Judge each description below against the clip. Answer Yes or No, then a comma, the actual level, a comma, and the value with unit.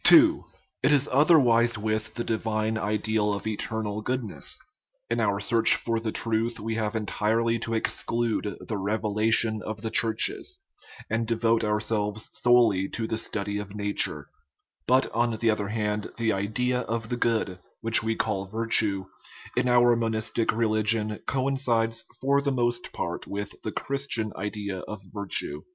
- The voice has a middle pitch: No, low, 110 Hz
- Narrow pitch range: Yes, narrow, 1.8 semitones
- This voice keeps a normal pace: Yes, average, 160 wpm